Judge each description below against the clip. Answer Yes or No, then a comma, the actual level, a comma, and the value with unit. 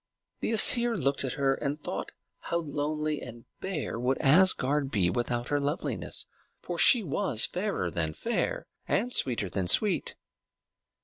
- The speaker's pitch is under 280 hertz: Yes, medium, 140 Hz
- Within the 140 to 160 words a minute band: Yes, average, 145 wpm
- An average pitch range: No, wide, 6.5 semitones